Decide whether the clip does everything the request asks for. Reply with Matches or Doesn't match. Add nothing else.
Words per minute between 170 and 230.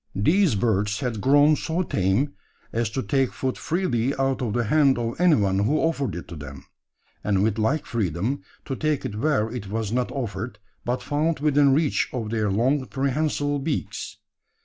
Matches